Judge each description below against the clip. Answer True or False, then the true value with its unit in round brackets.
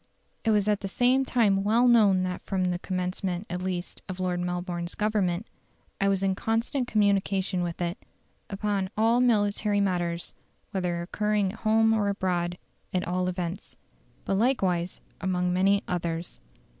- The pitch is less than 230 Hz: True (190 Hz)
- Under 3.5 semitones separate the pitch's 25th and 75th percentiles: True (2.8 semitones)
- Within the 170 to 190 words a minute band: False (155 wpm)